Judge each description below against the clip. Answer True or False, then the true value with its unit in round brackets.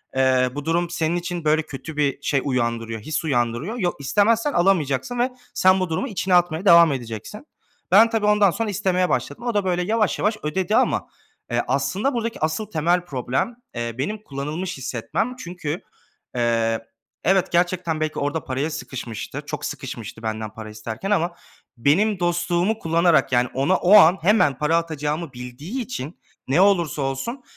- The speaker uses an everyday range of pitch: False (6.0 semitones)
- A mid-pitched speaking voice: True (165 Hz)